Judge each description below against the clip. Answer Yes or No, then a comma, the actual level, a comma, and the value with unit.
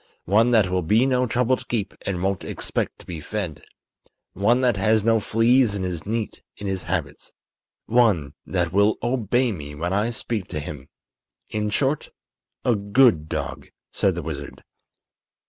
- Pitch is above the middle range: No, low, 105 Hz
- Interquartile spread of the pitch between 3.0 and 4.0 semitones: No, average, 4.6 semitones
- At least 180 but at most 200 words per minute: No, average, 165 wpm